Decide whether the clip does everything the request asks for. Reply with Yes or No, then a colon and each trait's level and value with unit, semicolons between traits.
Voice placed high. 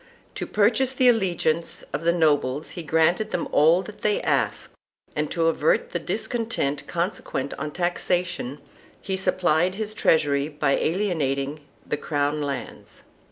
No: medium, 165 Hz